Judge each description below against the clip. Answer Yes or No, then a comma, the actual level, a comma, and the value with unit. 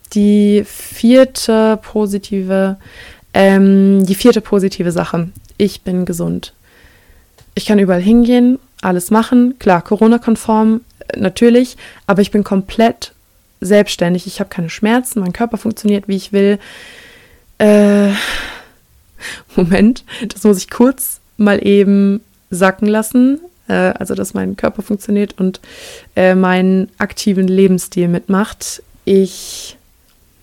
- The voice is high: Yes, high, 200 Hz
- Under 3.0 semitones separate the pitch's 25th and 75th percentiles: Yes, narrow, 2.6 semitones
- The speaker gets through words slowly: Yes, slow, 115 wpm